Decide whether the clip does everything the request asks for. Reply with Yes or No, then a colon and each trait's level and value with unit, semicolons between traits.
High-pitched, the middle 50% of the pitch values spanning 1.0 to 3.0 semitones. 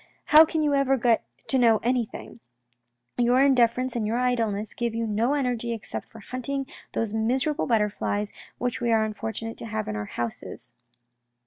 Yes: high, 235 Hz; average, 2.7 semitones